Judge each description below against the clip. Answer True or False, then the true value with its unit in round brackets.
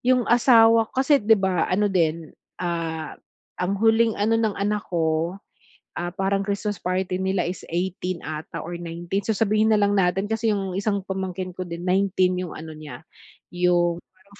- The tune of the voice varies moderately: True (3.0 semitones)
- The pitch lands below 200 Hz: True (190 Hz)